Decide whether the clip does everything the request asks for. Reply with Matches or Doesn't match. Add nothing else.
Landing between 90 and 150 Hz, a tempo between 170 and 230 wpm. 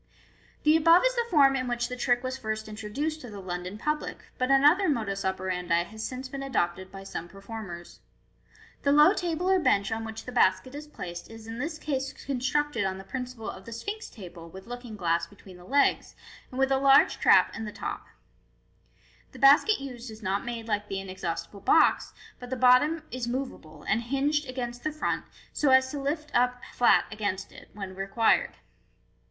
Doesn't match